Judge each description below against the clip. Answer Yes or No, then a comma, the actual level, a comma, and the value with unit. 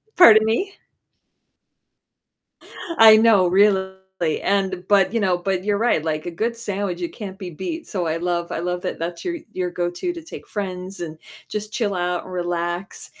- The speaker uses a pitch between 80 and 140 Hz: No, high, 190 Hz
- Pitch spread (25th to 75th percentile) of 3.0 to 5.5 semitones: Yes, average, 3.5 semitones